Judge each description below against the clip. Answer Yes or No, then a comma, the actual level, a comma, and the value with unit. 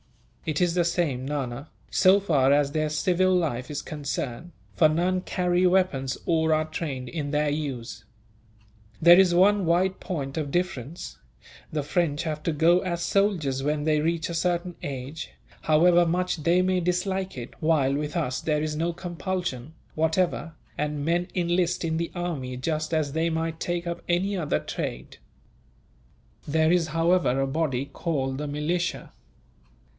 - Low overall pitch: No, medium, 160 Hz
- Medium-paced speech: Yes, average, 160 wpm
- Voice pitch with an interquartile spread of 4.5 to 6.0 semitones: No, average, 3.2 semitones